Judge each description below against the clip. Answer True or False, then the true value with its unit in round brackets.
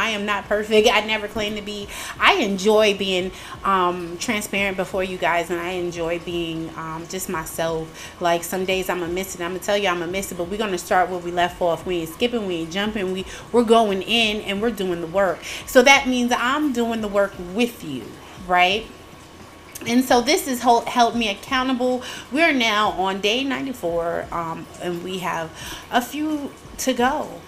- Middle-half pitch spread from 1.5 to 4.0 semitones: False (4.8 semitones)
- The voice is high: True (195 Hz)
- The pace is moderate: False (210 wpm)